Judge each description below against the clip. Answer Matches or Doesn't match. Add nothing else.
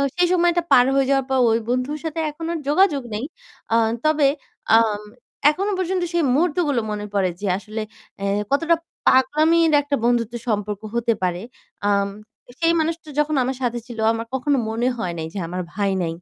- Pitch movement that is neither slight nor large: Doesn't match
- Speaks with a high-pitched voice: Matches